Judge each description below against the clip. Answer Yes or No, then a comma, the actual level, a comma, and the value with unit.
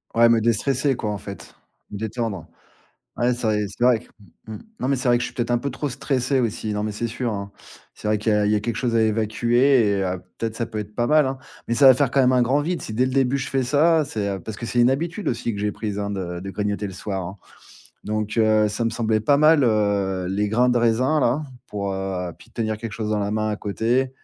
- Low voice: Yes, low, 115 Hz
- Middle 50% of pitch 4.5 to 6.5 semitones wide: No, average, 3.3 semitones